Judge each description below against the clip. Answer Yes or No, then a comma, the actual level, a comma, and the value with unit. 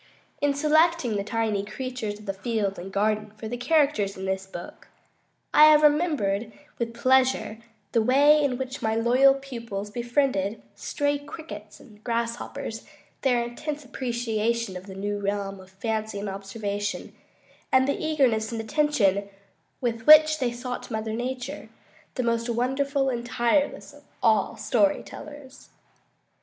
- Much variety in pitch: No, average, 4.6 semitones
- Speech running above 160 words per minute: No, average, 145 wpm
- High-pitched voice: Yes, high, 235 Hz